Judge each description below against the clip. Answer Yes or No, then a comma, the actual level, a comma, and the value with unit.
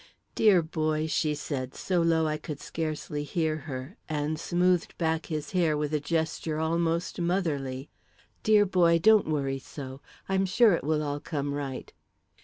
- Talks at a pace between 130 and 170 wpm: Yes, average, 160 wpm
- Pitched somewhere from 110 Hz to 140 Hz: No, medium, 155 Hz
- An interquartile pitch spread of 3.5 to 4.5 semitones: No, average, 2.7 semitones